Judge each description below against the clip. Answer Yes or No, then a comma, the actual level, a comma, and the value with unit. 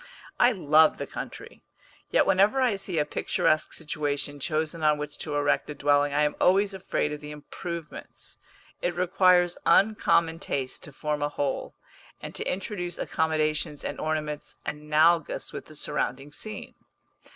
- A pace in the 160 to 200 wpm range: No, average, 150 wpm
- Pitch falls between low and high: Yes, medium, 155 Hz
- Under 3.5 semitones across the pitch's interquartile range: Yes, average, 3.1 semitones